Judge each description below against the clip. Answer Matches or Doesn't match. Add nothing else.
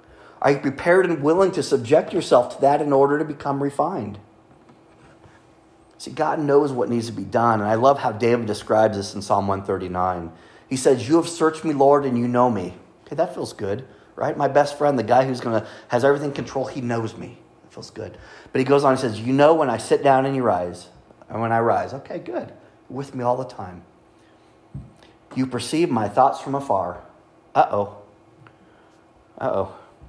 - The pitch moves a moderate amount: Matches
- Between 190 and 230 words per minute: Matches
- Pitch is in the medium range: Doesn't match